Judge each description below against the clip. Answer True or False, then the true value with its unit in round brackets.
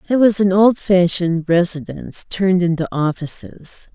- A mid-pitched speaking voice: True (180 Hz)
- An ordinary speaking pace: False (120 wpm)